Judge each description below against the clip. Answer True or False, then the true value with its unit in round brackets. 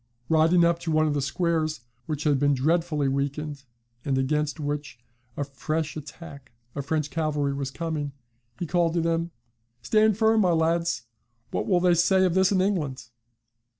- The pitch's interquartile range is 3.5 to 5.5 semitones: False (3.0 semitones)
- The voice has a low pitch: False (155 Hz)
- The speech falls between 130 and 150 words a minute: False (170 wpm)